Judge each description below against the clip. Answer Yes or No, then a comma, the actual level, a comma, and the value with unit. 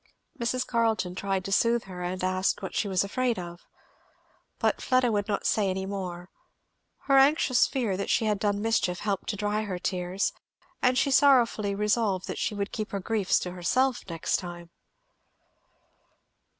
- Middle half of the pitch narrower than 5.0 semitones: Yes, average, 3.9 semitones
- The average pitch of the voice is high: Yes, high, 200 Hz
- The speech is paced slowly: No, average, 165 wpm